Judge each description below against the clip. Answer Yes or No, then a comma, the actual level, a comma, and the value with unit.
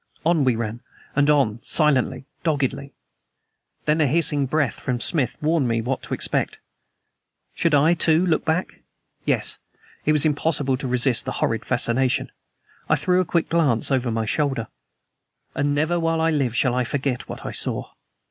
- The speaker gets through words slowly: No, average, 165 wpm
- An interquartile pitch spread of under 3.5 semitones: No, average, 3.9 semitones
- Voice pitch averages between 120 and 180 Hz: Yes, medium, 140 Hz